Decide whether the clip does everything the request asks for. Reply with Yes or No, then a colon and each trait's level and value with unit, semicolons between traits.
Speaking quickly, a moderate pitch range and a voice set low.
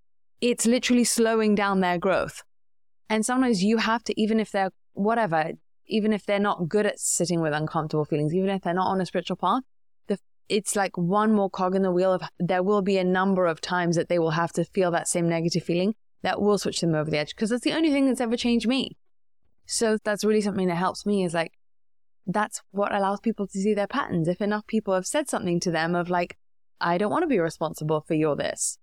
No: fast, 235 wpm; average, 3.9 semitones; high, 195 Hz